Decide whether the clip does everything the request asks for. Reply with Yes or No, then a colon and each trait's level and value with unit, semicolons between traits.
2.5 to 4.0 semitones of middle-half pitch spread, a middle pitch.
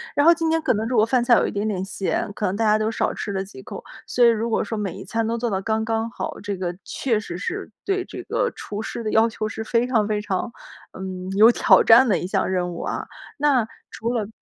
No: average, 2.9 semitones; high, 220 Hz